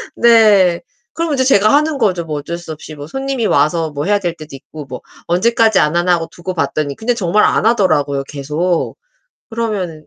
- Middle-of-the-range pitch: Yes, medium, 175 Hz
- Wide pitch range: Yes, wide, 6.4 semitones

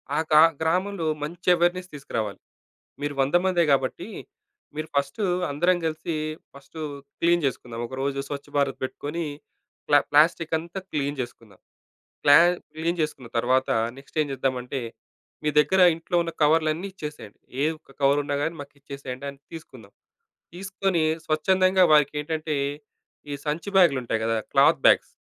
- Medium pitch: Yes, medium, 150 Hz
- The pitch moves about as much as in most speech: Yes, average, 3.5 semitones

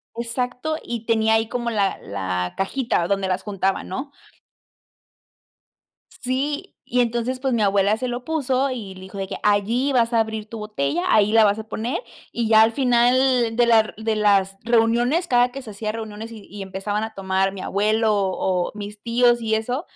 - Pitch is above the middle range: Yes, high, 220 Hz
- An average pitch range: Yes, average, 3.3 semitones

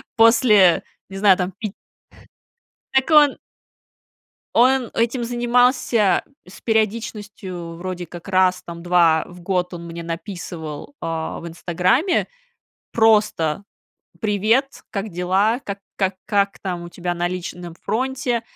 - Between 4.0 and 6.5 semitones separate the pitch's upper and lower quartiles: Yes, average, 4.6 semitones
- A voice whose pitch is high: Yes, high, 195 Hz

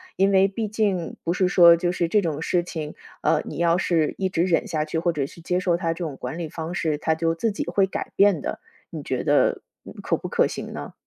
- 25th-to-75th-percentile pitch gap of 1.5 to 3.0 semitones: Yes, narrow, 2.5 semitones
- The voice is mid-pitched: Yes, medium, 170 Hz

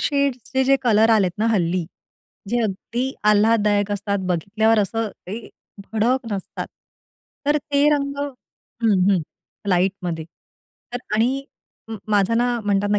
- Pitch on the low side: No, high, 220 Hz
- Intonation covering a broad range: No, average, 3.4 semitones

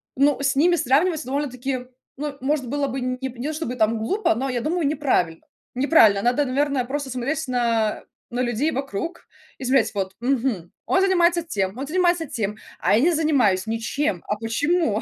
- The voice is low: No, very high, 265 Hz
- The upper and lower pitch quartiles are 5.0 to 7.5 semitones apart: No, average, 4.3 semitones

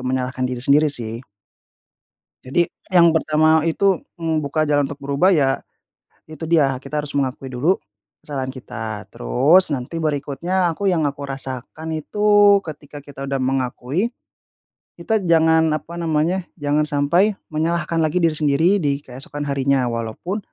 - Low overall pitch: No, medium, 150 Hz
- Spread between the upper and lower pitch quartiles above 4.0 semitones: No, average, 3.6 semitones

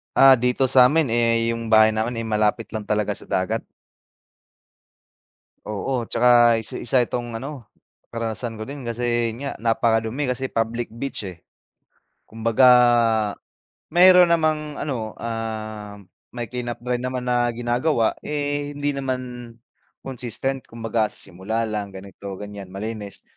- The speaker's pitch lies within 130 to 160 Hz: No, low, 115 Hz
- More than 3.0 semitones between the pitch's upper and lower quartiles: No, average, 2.7 semitones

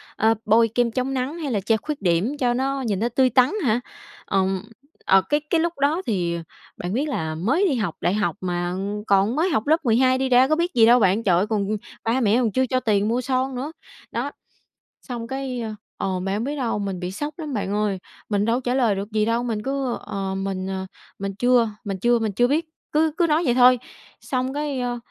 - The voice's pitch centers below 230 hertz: No, high, 235 Hz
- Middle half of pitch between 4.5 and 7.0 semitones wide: Yes, average, 4.8 semitones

